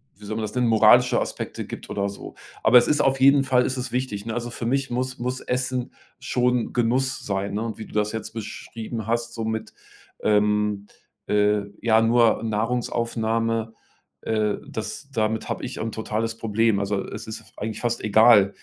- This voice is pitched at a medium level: No, low, 115 Hz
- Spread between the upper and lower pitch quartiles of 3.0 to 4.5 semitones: No, narrow, 2.4 semitones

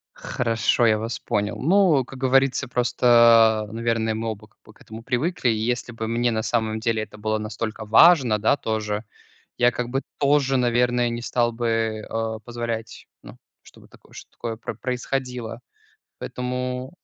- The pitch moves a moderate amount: No, narrow, 2.2 semitones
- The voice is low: Yes, low, 115 Hz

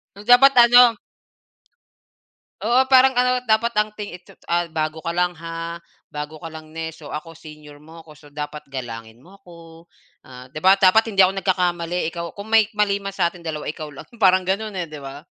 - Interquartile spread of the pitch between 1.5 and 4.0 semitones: No, average, 4.7 semitones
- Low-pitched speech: No, medium, 170 Hz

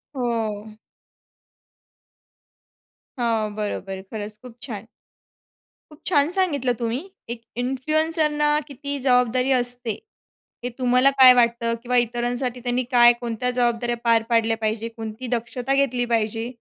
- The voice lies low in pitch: No, high, 245 Hz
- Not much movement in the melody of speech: Yes, narrow, 2.0 semitones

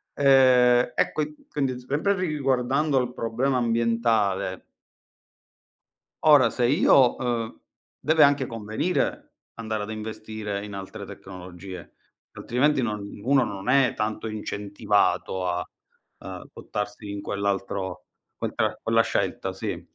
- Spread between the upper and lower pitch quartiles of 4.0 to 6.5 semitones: Yes, average, 4.5 semitones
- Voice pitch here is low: Yes, low, 115 Hz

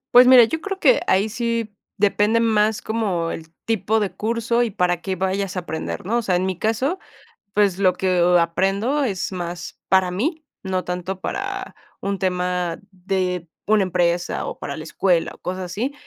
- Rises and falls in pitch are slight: No, average, 4.0 semitones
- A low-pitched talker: No, high, 195 Hz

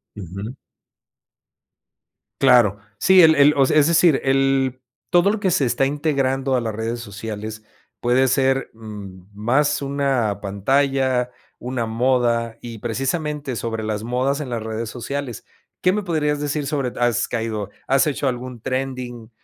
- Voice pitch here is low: Yes, low, 130 Hz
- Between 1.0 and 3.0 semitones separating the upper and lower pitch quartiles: No, average, 3.6 semitones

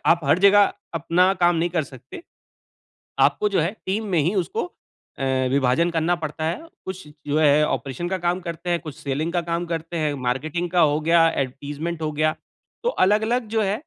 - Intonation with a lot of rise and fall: No, average, 2.7 semitones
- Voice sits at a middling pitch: Yes, medium, 170 Hz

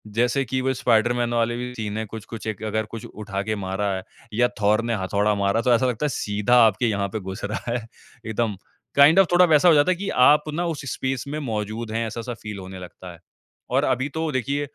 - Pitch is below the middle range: Yes, low, 115 Hz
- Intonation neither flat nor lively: Yes, average, 3.6 semitones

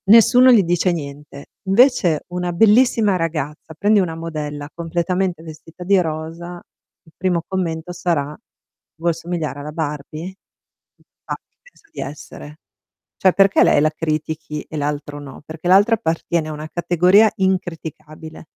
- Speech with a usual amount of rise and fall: Yes, average, 3.3 semitones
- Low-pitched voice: No, medium, 165 Hz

